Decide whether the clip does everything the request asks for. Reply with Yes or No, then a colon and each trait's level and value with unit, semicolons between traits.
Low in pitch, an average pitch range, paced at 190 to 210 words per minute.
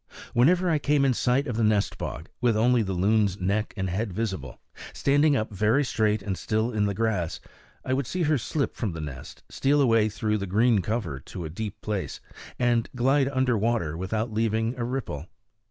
Yes: low, 110 Hz; average, 4.1 semitones; average, 200 wpm